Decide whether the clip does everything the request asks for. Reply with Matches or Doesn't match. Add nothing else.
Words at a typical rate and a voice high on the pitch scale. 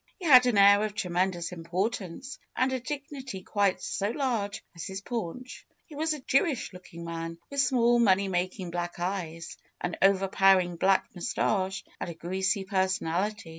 Matches